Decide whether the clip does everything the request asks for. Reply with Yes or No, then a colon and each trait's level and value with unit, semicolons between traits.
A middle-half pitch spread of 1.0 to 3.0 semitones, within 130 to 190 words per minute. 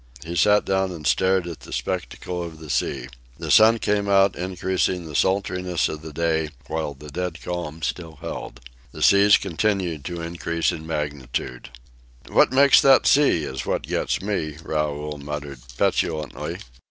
No: average, 3.8 semitones; average, 160 wpm